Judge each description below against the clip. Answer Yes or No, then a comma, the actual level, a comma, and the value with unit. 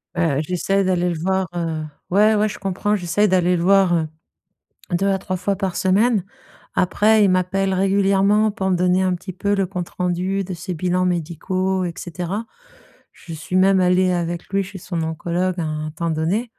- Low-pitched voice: No, medium, 185 Hz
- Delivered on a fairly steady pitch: Yes, narrow, 2.0 semitones